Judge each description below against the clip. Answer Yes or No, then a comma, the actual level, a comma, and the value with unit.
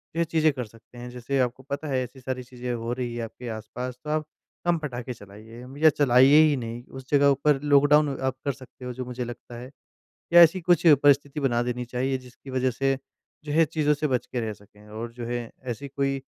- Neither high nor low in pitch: No, low, 130 Hz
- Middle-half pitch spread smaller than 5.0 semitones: Yes, average, 2.8 semitones